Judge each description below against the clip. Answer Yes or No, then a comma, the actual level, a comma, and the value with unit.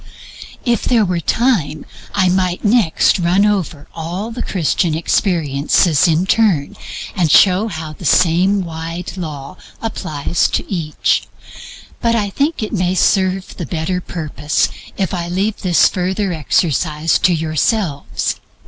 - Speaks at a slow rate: Yes, slow, 130 wpm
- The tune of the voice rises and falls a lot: No, average, 3.7 semitones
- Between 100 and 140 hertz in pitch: No, medium, 180 Hz